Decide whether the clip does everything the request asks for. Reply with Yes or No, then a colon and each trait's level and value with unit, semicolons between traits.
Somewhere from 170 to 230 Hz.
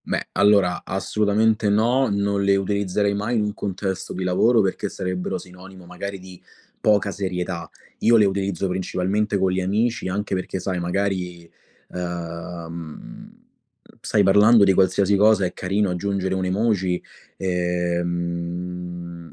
No: very low, 95 Hz